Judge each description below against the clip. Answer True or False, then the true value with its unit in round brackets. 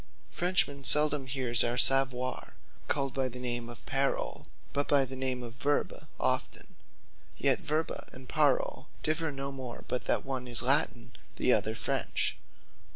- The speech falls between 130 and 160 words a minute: True (155 wpm)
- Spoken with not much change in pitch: True (2.2 semitones)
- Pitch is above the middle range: False (135 Hz)